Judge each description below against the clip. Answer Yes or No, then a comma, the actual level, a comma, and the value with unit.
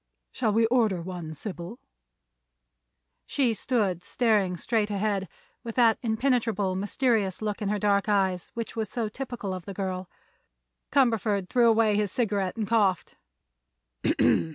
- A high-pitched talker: Yes, high, 210 Hz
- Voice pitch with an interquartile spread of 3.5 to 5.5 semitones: No, average, 3.1 semitones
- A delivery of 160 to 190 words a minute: No, slow, 135 wpm